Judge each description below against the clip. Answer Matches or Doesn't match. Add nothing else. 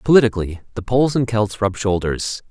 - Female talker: Doesn't match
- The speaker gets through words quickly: Doesn't match